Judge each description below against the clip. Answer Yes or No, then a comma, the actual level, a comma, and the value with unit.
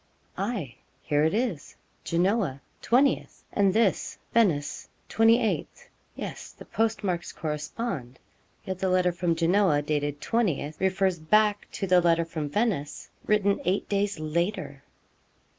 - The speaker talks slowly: Yes, slow, 125 wpm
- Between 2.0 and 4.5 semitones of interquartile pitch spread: No, average, 5.2 semitones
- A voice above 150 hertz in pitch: Yes, medium, 185 Hz